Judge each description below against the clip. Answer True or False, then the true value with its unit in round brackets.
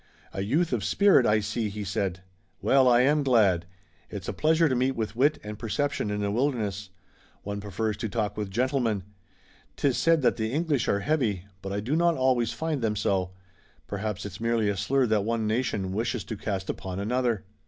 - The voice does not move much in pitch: False (4.3 semitones)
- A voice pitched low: True (110 Hz)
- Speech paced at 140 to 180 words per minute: False (195 wpm)